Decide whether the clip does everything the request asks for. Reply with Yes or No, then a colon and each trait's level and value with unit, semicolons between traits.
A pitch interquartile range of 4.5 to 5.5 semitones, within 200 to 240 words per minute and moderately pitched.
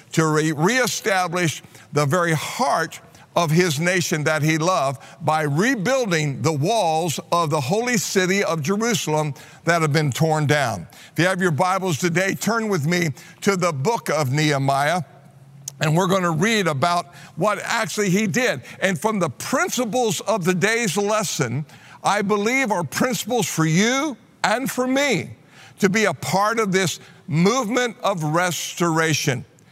No: average, 4.8 semitones; average, 155 wpm; medium, 175 Hz